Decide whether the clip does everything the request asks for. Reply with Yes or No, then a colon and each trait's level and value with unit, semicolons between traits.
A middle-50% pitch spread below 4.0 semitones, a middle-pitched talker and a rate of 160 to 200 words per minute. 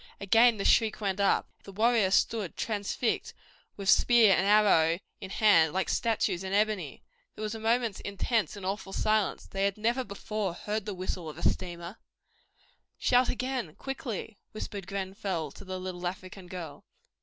No: average, 2.8 semitones; high, 200 Hz; average, 165 wpm